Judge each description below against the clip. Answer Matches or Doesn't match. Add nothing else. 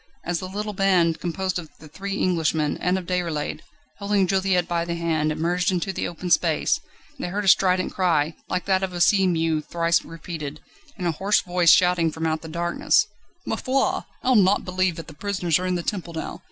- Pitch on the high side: Doesn't match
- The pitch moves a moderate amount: Doesn't match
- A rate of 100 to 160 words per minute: Doesn't match